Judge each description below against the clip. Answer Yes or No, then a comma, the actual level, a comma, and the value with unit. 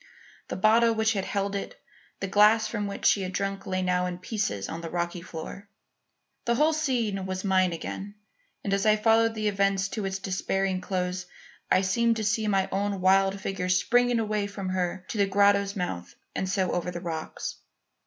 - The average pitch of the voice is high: Yes, high, 195 Hz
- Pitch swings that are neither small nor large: No, narrow, 2.3 semitones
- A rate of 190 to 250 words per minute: Yes, average, 195 wpm